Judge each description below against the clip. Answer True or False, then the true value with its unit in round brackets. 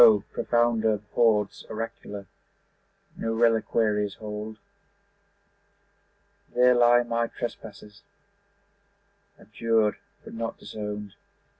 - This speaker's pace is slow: True (70 wpm)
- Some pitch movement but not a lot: False (1.8 semitones)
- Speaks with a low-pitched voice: True (110 Hz)